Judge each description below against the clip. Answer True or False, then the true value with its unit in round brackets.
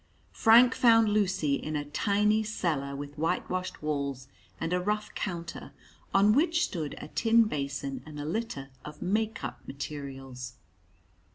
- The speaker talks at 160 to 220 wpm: False (145 wpm)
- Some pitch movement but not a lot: False (7.1 semitones)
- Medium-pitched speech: True (165 Hz)